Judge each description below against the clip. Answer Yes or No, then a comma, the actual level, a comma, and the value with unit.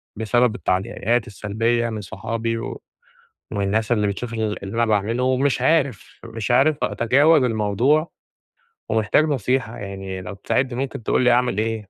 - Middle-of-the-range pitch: No, low, 115 Hz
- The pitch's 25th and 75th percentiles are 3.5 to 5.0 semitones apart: No, average, 3.1 semitones